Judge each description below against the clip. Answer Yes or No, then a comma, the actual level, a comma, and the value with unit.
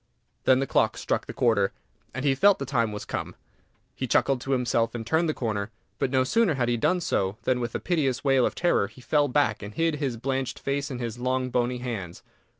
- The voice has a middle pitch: No, low, 130 Hz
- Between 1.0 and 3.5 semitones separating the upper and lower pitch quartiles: Yes, average, 2.9 semitones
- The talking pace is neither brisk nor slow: No, fast, 230 wpm